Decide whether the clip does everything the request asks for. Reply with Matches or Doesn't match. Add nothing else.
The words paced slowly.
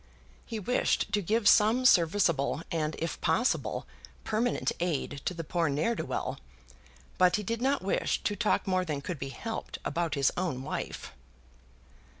Doesn't match